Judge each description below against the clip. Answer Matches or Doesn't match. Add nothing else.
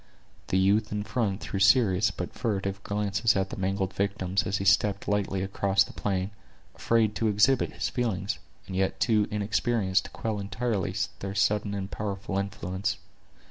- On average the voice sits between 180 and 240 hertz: Doesn't match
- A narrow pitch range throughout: Matches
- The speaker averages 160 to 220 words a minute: Matches